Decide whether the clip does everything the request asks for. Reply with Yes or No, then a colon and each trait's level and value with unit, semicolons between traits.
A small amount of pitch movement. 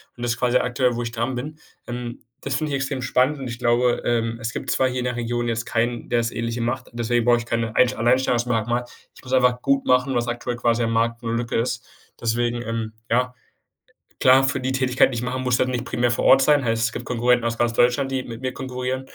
Yes: narrow, 1.5 semitones